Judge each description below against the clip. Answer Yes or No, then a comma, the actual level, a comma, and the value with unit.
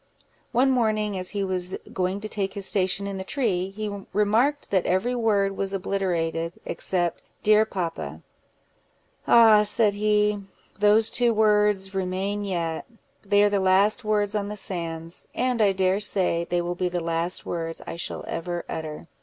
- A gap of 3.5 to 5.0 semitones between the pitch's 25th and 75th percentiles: No, average, 2.7 semitones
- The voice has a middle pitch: No, high, 195 Hz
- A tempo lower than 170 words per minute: Yes, average, 160 wpm